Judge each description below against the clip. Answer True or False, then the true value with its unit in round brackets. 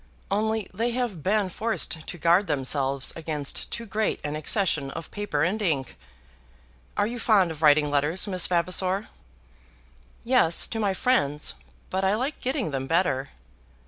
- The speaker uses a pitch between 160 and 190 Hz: True (185 Hz)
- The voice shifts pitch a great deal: True (6.3 semitones)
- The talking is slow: False (150 wpm)